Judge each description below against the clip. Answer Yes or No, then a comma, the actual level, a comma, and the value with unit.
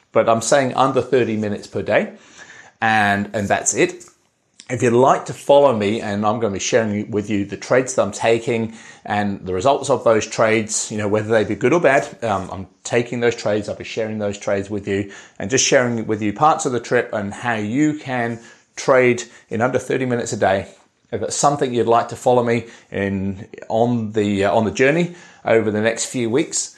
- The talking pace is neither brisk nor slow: No, fast, 215 wpm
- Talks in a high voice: No, low, 110 Hz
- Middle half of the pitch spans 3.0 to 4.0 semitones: No, narrow, 2.4 semitones